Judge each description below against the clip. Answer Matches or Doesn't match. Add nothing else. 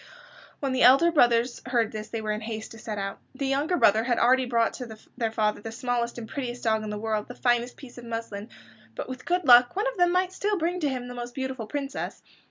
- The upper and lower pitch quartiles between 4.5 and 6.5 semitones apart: Doesn't match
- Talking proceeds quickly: Matches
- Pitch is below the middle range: Doesn't match